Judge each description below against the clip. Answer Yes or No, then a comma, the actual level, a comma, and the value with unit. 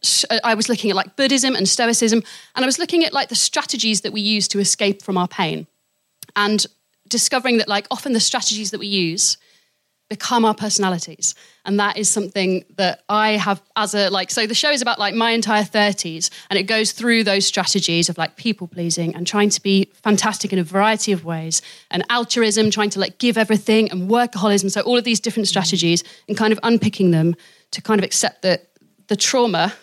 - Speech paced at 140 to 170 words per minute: No, fast, 205 wpm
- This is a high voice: Yes, high, 210 Hz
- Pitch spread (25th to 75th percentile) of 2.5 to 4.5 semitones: Yes, average, 2.9 semitones